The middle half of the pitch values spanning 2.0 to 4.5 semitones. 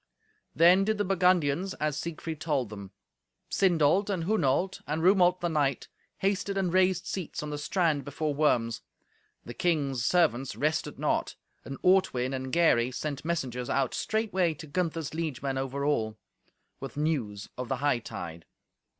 No: average, 5.1 semitones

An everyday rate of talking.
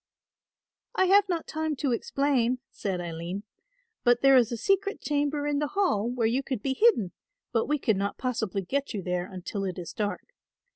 Yes: average, 190 wpm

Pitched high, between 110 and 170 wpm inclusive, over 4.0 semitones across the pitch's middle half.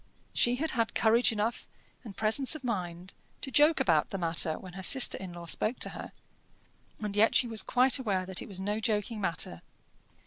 No: high, 210 Hz; average, 200 wpm; average, 4.5 semitones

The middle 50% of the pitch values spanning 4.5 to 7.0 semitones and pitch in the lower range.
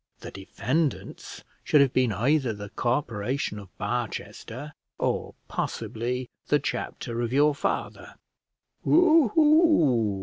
Yes: average, 5.1 semitones; low, 125 Hz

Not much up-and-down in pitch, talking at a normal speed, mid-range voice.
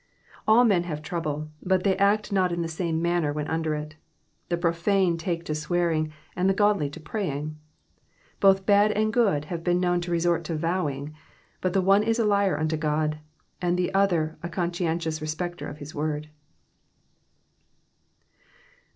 No: average, 3.5 semitones; average, 170 wpm; medium, 170 Hz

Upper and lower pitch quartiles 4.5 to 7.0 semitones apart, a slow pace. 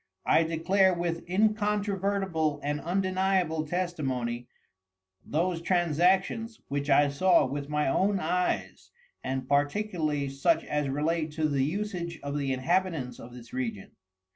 Yes: average, 4.8 semitones; slow, 125 wpm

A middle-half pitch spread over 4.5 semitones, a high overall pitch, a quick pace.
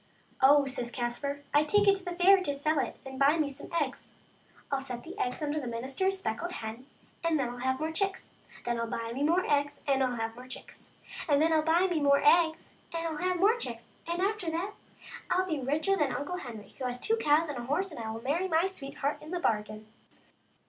Yes: average, 5.0 semitones; very high, 290 Hz; fast, 230 wpm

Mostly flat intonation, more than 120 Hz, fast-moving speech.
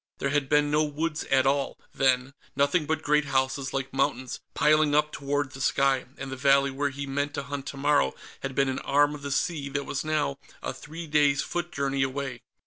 Yes: narrow, 1.5 semitones; medium, 140 Hz; fast, 210 wpm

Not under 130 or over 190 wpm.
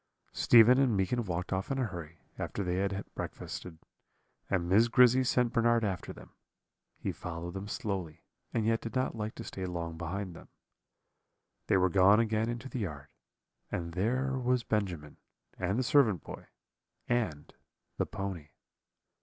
Yes: average, 160 wpm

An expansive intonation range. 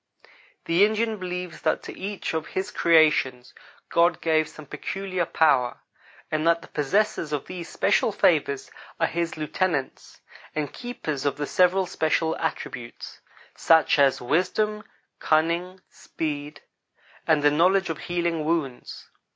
No: average, 3.4 semitones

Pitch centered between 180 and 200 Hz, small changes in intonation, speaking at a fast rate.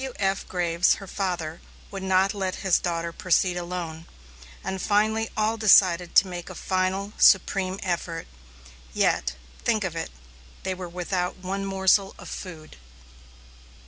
No: medium, 185 Hz; narrow, 2.1 semitones; average, 140 wpm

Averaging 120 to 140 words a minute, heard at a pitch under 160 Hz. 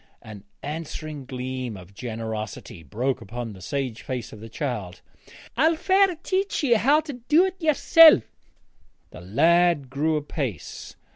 Yes: slow, 135 wpm; low, 135 Hz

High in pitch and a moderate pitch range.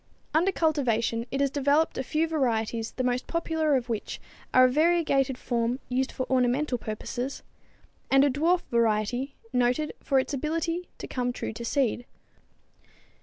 Yes: very high, 265 Hz; average, 3.9 semitones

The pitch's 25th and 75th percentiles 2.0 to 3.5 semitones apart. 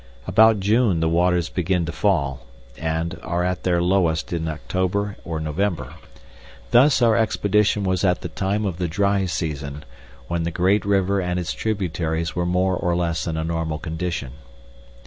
Yes: average, 3.2 semitones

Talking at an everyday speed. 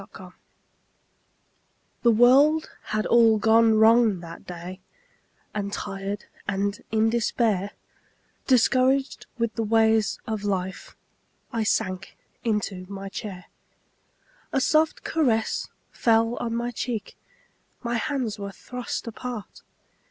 No: slow, 115 wpm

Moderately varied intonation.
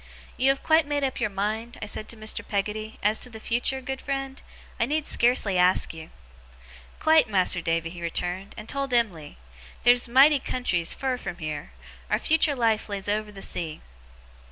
No: wide, 5.7 semitones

